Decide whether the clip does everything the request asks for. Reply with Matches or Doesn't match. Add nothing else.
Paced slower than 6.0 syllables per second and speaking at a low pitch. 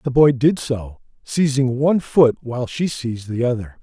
Matches